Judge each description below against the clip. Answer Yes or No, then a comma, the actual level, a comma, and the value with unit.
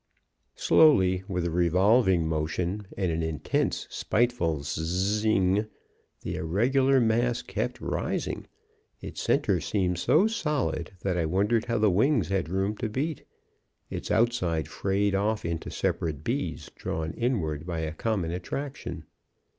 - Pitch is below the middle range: Yes, very low, 95 Hz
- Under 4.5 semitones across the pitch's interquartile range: No, wide, 5.5 semitones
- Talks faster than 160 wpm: No, slow, 135 wpm